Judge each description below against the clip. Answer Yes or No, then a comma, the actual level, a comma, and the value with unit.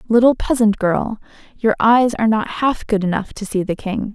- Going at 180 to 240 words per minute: Yes, average, 200 wpm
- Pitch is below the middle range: No, high, 215 Hz